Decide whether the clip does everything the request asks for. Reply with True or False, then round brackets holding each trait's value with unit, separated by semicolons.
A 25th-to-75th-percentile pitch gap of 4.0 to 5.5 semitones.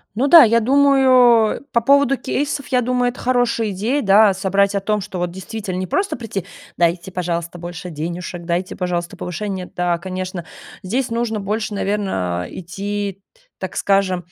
True (4.8 semitones)